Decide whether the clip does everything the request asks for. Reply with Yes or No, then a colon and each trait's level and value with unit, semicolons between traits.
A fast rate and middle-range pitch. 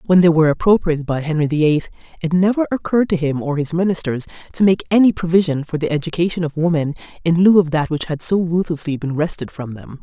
Yes: fast, 220 wpm; medium, 165 Hz